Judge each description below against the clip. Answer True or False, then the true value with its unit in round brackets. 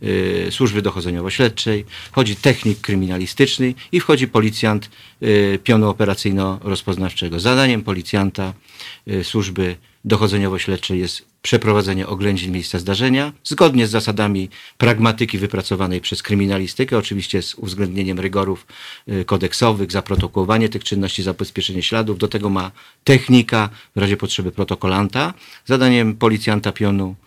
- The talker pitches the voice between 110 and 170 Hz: False (100 Hz)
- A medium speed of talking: False (105 wpm)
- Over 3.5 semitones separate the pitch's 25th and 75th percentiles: False (2.9 semitones)